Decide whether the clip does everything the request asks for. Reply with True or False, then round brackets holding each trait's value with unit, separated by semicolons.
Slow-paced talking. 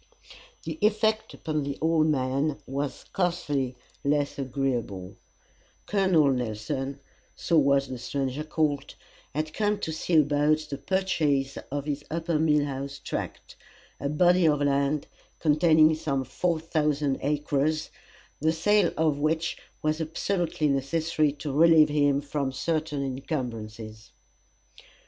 True (125 wpm)